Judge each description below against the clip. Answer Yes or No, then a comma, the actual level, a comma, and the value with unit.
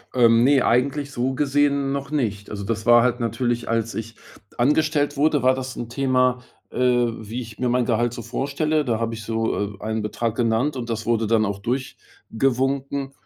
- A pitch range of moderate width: Yes, average, 3.1 semitones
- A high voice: No, low, 120 Hz